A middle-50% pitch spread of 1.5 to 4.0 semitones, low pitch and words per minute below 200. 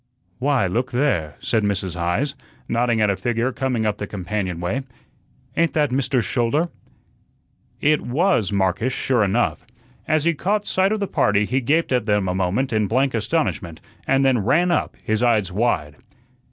No: average, 5.2 semitones; low, 120 Hz; average, 170 wpm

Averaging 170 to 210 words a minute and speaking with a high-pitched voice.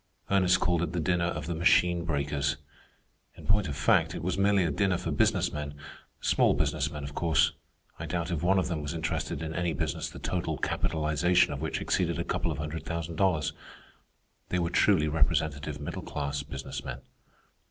No: average, 190 wpm; very low, 80 Hz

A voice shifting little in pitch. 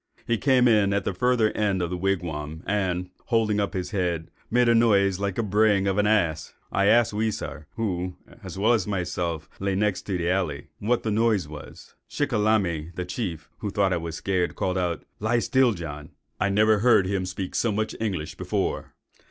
No: average, 3.6 semitones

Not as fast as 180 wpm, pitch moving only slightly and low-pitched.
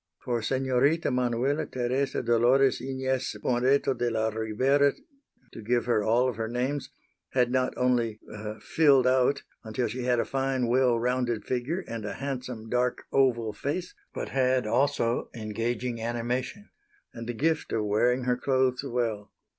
Yes: average, 150 wpm; narrow, 2.2 semitones; low, 125 Hz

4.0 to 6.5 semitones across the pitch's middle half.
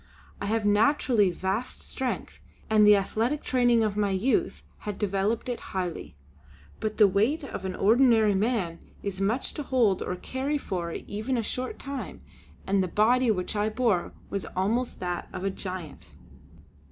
Yes: average, 4.3 semitones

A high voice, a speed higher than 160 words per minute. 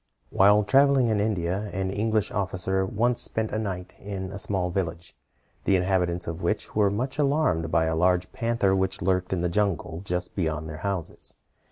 No: very low, 95 Hz; average, 180 wpm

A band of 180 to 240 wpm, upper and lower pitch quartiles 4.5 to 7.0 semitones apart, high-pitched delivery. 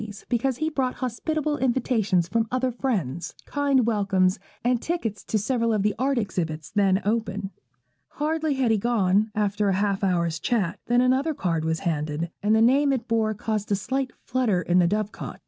Yes: average, 185 wpm; average, 4.8 semitones; high, 220 Hz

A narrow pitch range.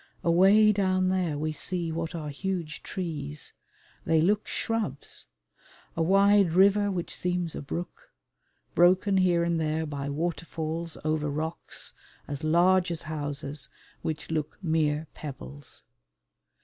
No: average, 3.3 semitones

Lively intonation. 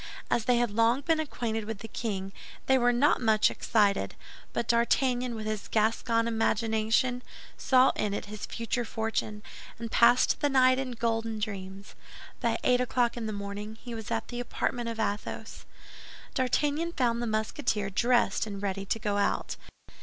No: narrow, 2.5 semitones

